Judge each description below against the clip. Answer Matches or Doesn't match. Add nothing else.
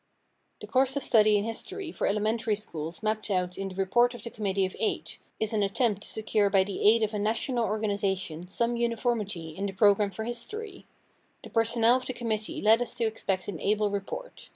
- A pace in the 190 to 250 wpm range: Matches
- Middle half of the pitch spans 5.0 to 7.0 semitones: Doesn't match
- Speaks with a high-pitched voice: Matches